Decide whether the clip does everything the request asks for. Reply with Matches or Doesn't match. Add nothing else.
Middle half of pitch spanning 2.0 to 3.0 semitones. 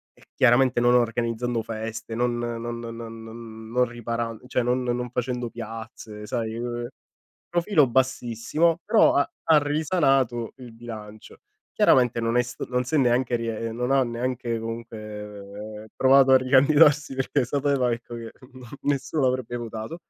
Matches